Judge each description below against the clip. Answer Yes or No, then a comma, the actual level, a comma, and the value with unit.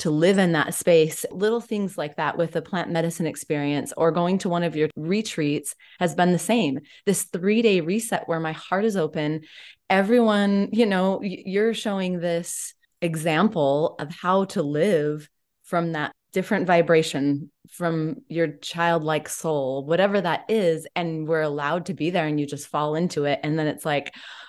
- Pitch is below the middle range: No, medium, 170 Hz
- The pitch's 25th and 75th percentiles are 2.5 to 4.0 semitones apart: Yes, average, 3.7 semitones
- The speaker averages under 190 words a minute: Yes, average, 175 wpm